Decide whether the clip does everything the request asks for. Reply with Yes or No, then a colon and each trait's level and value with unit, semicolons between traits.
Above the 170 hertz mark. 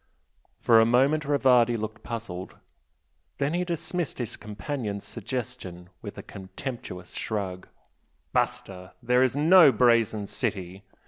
No: low, 115 Hz